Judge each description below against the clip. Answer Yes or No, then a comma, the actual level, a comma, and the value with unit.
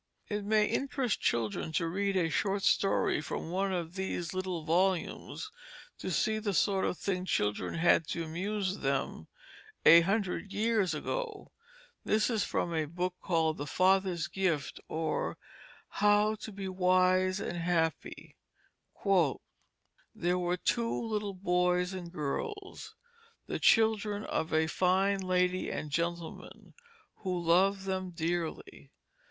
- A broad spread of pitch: No, average, 3.0 semitones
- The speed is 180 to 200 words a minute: No, slow, 135 wpm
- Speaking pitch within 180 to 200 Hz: Yes, medium, 185 Hz